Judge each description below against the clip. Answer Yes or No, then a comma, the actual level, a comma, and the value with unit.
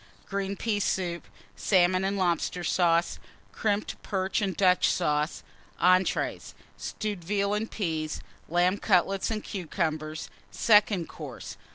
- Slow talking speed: Yes, slow, 120 wpm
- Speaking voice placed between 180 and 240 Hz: Yes, medium, 185 Hz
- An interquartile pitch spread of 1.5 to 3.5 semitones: Yes, average, 2.8 semitones